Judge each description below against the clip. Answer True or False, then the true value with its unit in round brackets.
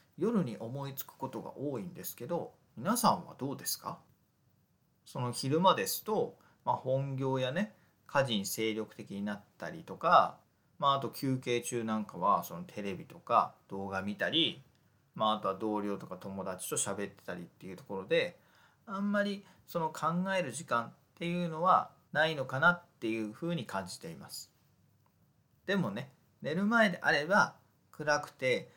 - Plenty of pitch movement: True (8.2 semitones)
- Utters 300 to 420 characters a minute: True (310 characters per minute)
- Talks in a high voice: False (135 Hz)